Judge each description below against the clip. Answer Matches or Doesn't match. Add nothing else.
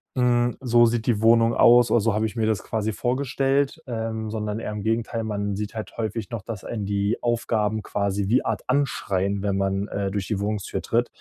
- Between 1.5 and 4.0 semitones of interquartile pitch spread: Matches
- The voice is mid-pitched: Doesn't match